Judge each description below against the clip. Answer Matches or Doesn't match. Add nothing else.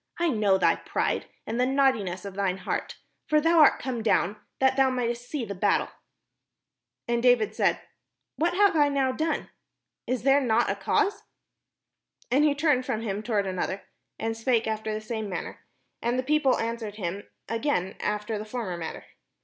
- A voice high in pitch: Matches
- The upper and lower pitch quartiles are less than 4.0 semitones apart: Doesn't match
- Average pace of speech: Matches